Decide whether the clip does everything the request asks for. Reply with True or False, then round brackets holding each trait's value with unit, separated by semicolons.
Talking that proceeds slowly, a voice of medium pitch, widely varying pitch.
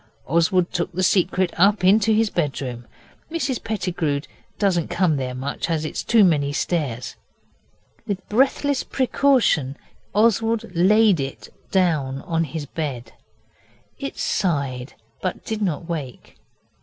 True (120 wpm; 175 Hz; 6.3 semitones)